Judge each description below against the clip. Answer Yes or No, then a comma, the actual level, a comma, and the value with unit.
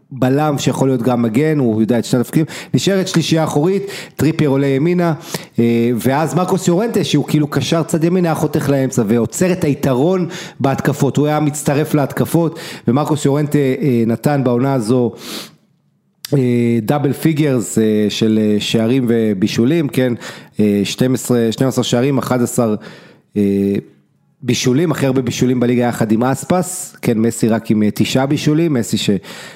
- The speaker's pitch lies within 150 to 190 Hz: No, low, 135 Hz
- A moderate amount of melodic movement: Yes, average, 4.5 semitones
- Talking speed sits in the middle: Yes, average, 140 wpm